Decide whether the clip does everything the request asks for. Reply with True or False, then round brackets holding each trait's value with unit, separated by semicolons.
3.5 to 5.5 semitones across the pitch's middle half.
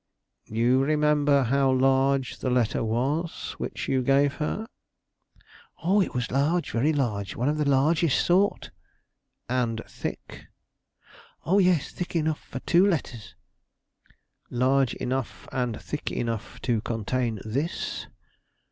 True (3.9 semitones)